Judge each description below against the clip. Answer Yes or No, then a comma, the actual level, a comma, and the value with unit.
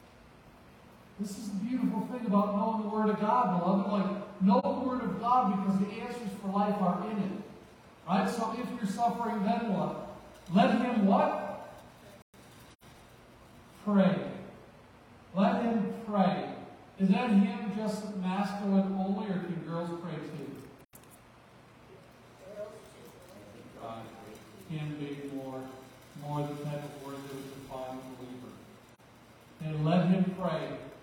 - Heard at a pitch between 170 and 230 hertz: Yes, high, 190 Hz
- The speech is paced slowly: Yes, slow, 130 wpm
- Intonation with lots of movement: Yes, wide, 6.4 semitones